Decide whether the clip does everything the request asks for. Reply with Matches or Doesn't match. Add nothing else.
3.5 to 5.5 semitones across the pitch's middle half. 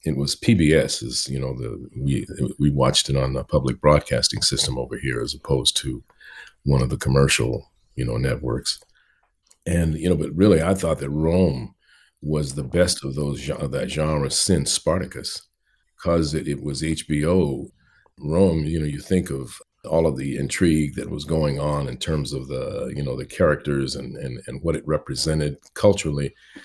Doesn't match